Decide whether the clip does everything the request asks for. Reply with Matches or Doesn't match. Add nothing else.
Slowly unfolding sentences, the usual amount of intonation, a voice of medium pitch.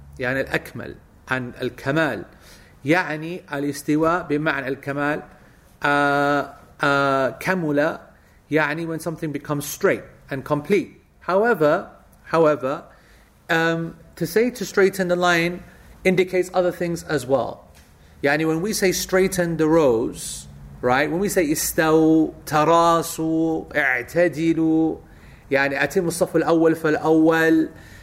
Matches